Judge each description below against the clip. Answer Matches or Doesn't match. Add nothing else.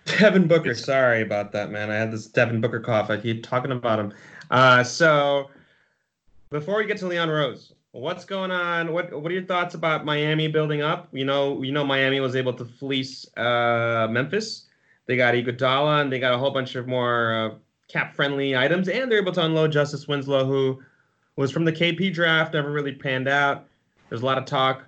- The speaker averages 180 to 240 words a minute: Matches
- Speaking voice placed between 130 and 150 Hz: Matches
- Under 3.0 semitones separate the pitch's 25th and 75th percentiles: Doesn't match